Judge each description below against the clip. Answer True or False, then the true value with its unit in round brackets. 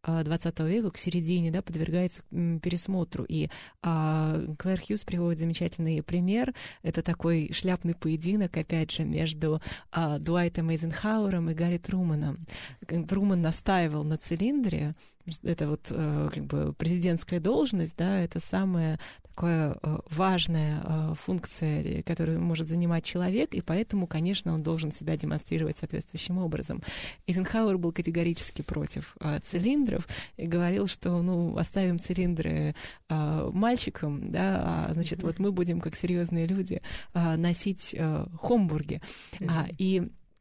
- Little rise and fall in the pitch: True (2.2 semitones)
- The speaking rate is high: False (120 wpm)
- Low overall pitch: False (170 Hz)